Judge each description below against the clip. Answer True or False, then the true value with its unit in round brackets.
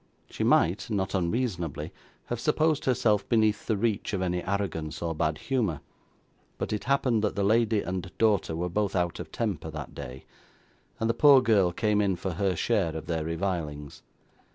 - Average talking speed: True (175 wpm)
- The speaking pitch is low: True (100 Hz)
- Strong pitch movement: False (4.9 semitones)